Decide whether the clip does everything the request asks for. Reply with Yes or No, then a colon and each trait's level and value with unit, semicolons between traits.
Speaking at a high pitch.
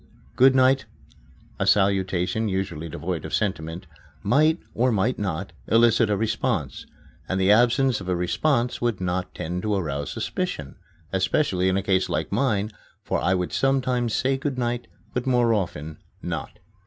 No: low, 105 Hz